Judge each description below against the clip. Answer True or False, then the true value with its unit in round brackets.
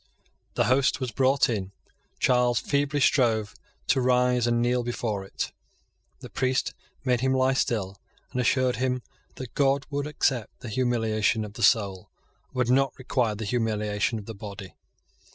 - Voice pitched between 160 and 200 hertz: False (120 Hz)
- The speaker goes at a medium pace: True (160 wpm)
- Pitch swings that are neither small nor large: True (3.1 semitones)